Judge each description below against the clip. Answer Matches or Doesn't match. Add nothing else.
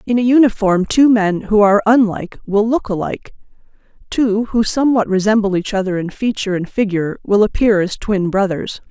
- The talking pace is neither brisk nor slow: Matches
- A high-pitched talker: Matches